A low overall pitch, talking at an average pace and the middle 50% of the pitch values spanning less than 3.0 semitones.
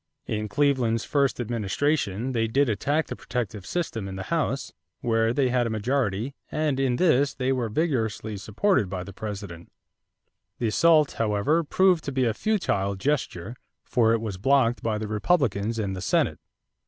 No: low, 115 Hz; average, 165 wpm; average, 4.9 semitones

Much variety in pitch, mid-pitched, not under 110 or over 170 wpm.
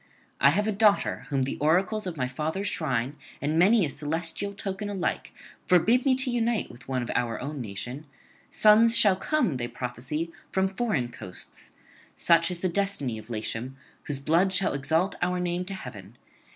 No: wide, 6.8 semitones; medium, 165 Hz; average, 180 wpm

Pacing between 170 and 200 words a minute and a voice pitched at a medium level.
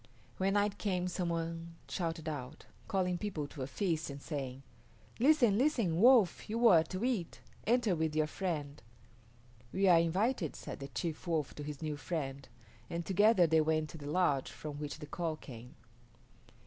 Yes: average, 175 wpm; medium, 165 Hz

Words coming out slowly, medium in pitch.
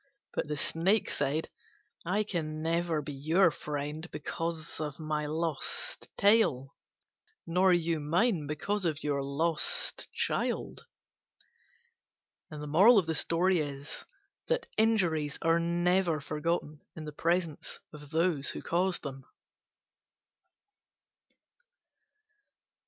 Yes: slow, 90 wpm; medium, 160 Hz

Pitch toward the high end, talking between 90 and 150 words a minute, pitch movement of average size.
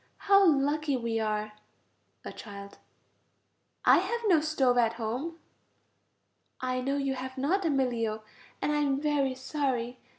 Yes: very high, 265 Hz; slow, 135 wpm; average, 4.0 semitones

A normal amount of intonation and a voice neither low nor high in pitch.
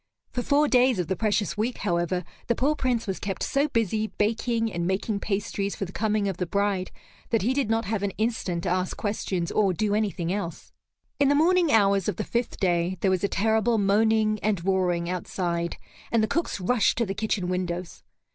No: average, 3.4 semitones; high, 205 Hz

